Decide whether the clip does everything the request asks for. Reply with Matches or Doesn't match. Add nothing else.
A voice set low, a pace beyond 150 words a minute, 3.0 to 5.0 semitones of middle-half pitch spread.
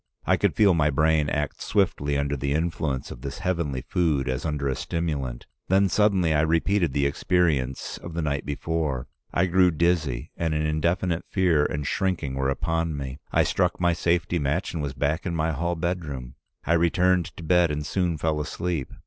Matches